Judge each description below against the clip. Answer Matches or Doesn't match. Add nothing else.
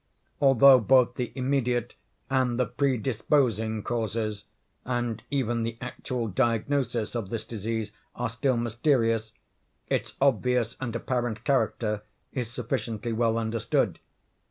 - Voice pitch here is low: Matches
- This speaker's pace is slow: Matches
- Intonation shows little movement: Matches